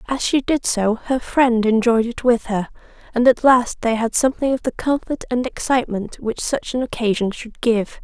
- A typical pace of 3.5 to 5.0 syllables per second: Yes, 4.9 syllables/s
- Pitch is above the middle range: Yes, high, 240 Hz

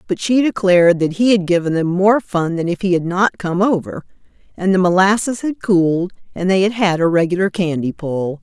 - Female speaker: Yes, female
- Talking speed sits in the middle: No, fast, 215 wpm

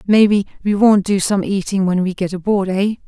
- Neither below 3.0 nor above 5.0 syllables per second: No, 5.3 syllables/s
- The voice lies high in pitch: Yes, high, 195 Hz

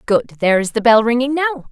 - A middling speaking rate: No, fast, 245 wpm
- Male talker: No, female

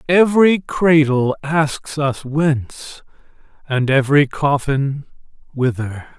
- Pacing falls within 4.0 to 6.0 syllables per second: No, 3.6 syllables/s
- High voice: No, medium, 145 Hz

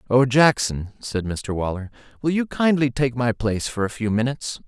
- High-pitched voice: No, low, 120 Hz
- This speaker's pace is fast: No, average, 190 wpm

